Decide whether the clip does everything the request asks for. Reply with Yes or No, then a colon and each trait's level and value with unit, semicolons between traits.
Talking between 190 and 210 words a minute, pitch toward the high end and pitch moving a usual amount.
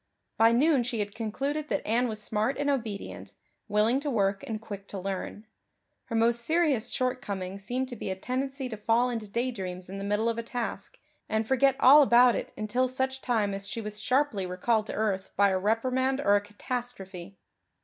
Yes: average, 195 wpm; high, 225 Hz; average, 3.8 semitones